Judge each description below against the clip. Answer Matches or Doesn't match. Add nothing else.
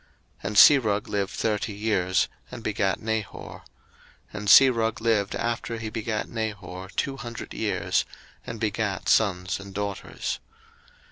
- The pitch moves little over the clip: Matches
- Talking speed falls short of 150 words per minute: Matches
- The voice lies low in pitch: Matches